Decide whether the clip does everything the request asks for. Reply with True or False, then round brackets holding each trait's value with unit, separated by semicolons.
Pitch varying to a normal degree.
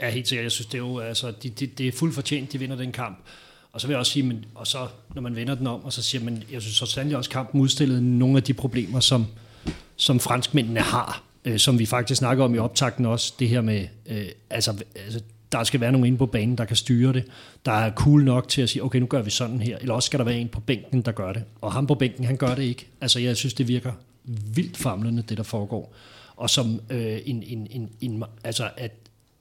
False (2.3 semitones)